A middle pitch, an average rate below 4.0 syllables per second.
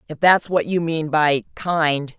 Yes: medium, 160 Hz; 3.7 syllables/s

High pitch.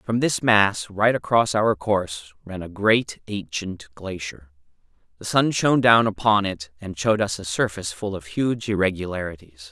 No: low, 100 Hz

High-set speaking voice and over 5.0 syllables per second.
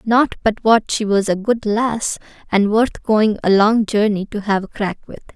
No: high, 215 Hz; 4.5 syllables/s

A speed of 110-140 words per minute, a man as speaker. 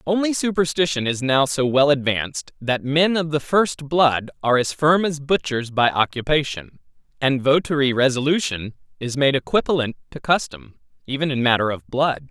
No: average, 160 wpm; male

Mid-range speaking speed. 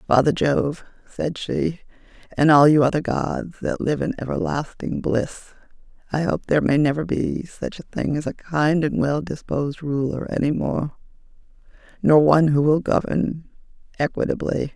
Yes: average, 155 wpm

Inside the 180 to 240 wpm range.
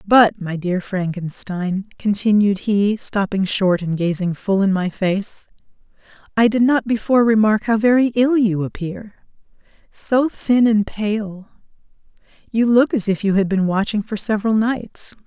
No: average, 155 wpm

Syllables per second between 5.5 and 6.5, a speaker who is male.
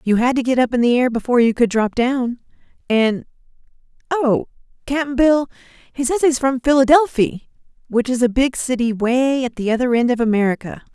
No: 5.6 syllables/s; female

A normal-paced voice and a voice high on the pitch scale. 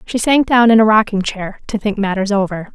No: fast, 240 wpm; high, 210 Hz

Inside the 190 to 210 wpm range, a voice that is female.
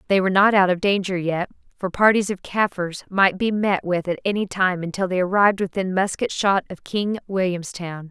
Yes: average, 200 wpm; female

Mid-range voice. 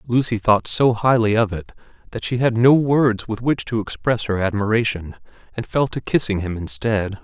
No: low, 110 Hz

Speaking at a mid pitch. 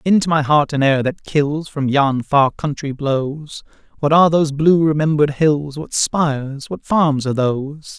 Yes: medium, 150 Hz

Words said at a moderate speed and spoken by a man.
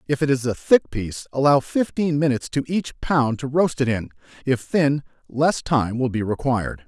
Yes: average, 190 wpm; male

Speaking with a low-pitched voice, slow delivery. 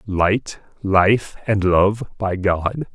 Yes: low, 100 Hz; slow, 120 wpm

